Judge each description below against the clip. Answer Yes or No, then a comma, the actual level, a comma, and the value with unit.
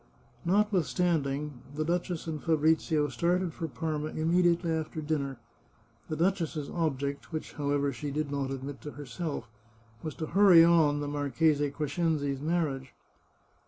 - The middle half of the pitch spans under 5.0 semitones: Yes, average, 2.8 semitones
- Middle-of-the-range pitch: Yes, medium, 155 Hz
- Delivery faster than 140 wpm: No, slow, 135 wpm